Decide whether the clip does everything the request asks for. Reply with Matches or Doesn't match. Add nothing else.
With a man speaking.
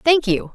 Doesn't match